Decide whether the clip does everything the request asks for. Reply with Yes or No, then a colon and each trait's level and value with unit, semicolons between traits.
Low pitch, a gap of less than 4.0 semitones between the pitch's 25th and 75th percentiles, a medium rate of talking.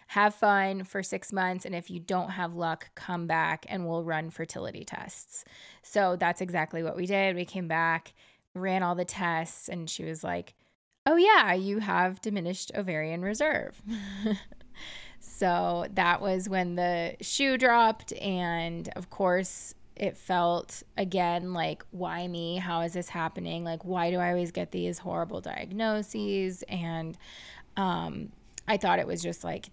No: medium, 180 Hz; narrow, 2.6 semitones; average, 160 wpm